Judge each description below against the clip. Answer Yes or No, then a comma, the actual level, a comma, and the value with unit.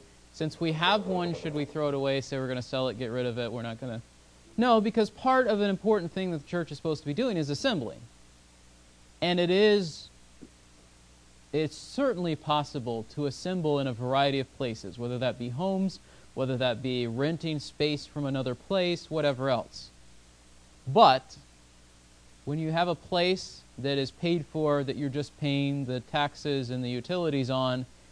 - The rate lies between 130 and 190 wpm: Yes, average, 185 wpm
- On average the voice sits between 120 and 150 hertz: Yes, medium, 140 Hz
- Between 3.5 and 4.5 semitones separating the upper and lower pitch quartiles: No, average, 5.1 semitones